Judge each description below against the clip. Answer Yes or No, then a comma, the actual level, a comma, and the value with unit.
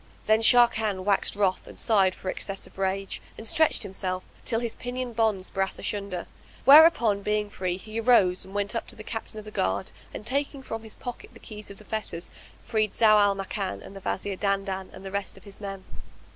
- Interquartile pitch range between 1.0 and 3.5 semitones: Yes, narrow, 2.5 semitones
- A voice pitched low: No, high, 205 Hz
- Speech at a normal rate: No, fast, 210 wpm